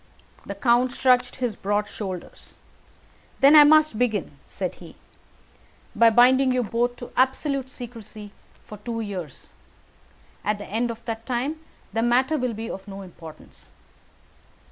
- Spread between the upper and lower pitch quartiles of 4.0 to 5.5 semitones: No, average, 3.6 semitones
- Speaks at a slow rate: No, average, 145 wpm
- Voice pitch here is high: Yes, high, 235 Hz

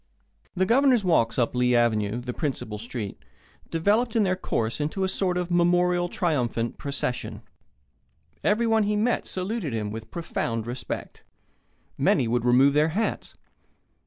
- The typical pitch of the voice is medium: Yes, medium, 155 Hz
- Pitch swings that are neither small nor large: No, wide, 8.0 semitones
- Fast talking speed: No, average, 140 wpm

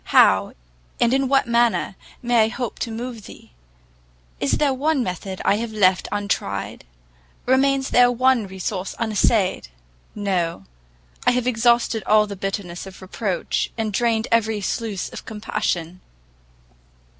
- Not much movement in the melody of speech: No, average, 3.7 semitones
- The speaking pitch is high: Yes, high, 220 Hz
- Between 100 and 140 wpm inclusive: Yes, slow, 135 wpm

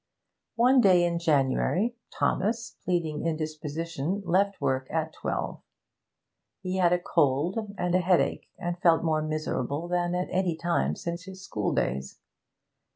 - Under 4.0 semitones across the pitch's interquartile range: Yes, average, 2.9 semitones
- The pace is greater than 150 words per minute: No, average, 140 wpm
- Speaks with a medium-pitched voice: Yes, medium, 170 Hz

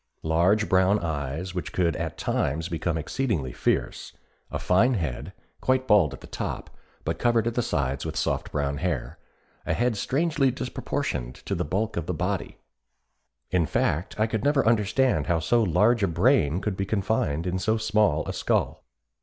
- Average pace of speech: Yes, average, 175 wpm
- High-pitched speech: No, very low, 95 Hz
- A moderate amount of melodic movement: No, wide, 5.7 semitones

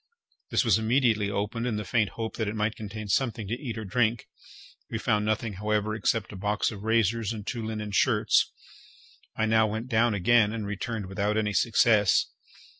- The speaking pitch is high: No, low, 110 Hz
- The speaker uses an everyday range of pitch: No, narrow, 1.6 semitones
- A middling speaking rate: Yes, average, 190 wpm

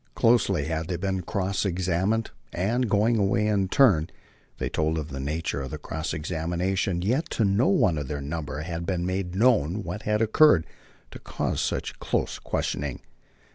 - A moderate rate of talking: Yes, average, 175 wpm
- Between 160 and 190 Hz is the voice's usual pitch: No, very low, 90 Hz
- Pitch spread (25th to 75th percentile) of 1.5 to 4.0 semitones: No, average, 4.6 semitones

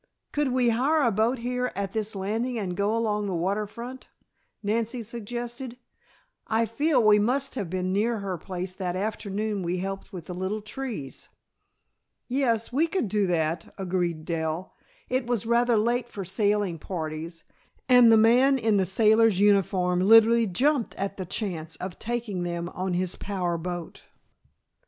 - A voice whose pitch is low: No, high, 210 Hz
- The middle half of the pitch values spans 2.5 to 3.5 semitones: No, average, 4.3 semitones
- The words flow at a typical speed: Yes, average, 160 wpm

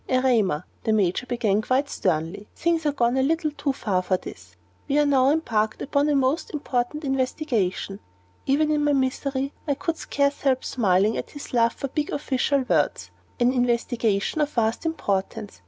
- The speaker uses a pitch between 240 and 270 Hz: Yes, very high, 260 Hz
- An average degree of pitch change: Yes, average, 4.8 semitones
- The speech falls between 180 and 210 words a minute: No, average, 170 wpm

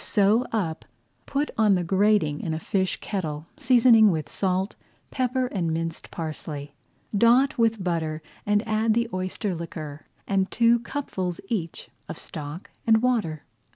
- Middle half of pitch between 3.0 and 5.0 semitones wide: No, wide, 5.6 semitones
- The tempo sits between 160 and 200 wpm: No, average, 145 wpm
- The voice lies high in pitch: Yes, high, 195 Hz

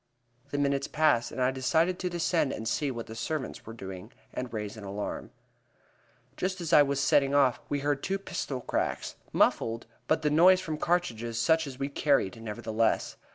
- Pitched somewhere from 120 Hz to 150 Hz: Yes, medium, 140 Hz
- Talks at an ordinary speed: Yes, average, 185 wpm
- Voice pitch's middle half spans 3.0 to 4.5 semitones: No, wide, 5.4 semitones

